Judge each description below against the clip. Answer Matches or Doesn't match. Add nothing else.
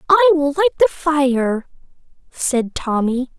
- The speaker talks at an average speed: Doesn't match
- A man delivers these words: Doesn't match